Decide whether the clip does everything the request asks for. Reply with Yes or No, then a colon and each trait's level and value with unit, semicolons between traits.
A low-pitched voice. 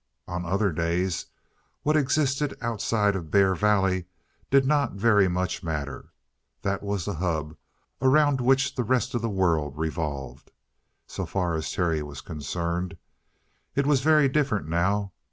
Yes: very low, 95 Hz